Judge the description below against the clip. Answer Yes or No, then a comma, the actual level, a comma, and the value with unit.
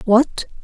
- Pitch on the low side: No, high, 235 Hz